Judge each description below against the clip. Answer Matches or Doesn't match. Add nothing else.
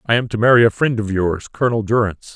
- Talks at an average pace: Doesn't match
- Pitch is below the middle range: Matches